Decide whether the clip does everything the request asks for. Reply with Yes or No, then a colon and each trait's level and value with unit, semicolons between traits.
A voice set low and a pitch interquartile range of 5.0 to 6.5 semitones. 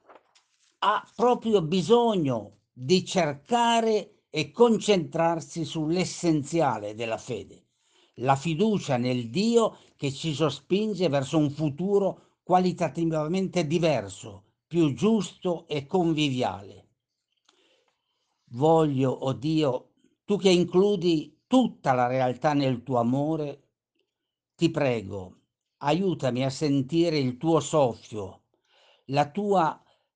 No: medium, 160 Hz; wide, 5.6 semitones